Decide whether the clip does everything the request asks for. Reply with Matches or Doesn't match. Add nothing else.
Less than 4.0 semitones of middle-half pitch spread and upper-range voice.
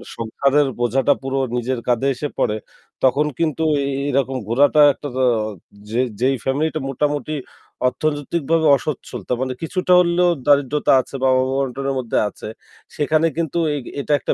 Doesn't match